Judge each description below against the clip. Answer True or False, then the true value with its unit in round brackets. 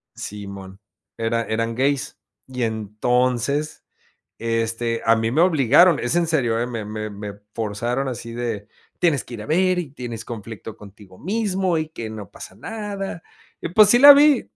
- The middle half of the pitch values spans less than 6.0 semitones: False (6.5 semitones)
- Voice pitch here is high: False (120 Hz)